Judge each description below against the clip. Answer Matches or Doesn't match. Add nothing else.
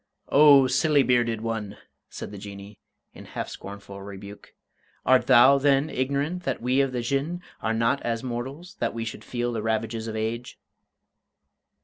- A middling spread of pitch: Matches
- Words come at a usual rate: Matches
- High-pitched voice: Doesn't match